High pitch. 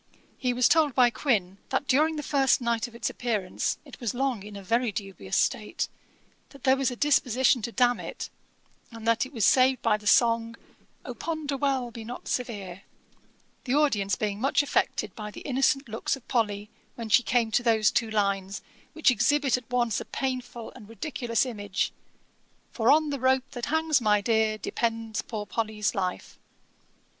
Yes: high, 235 Hz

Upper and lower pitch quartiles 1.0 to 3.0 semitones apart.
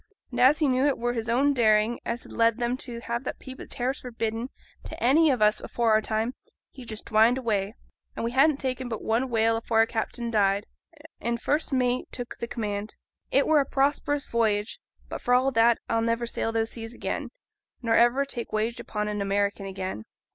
Yes: narrow, 2.5 semitones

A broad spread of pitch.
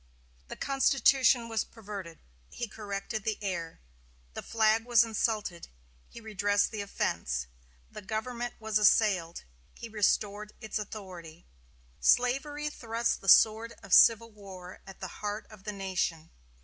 No: average, 2.9 semitones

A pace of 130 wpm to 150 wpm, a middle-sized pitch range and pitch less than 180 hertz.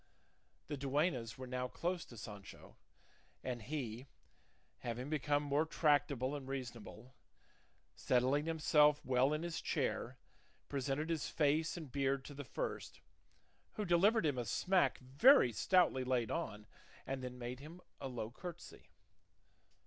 Yes: slow, 135 wpm; average, 3.5 semitones; low, 135 Hz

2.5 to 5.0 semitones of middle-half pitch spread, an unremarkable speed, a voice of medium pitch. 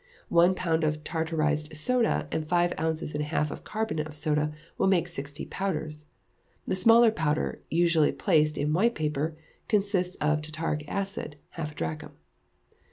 Yes: average, 3.1 semitones; average, 160 wpm; medium, 160 Hz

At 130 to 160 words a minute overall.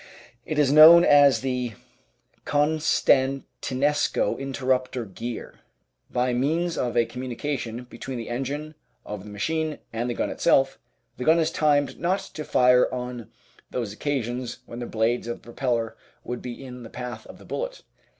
Yes: average, 155 wpm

